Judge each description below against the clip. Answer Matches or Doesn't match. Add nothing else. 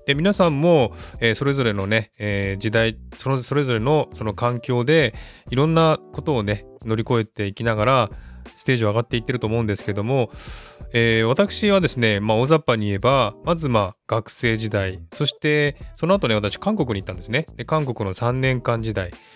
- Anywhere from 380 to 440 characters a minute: Doesn't match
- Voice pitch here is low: Matches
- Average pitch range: Matches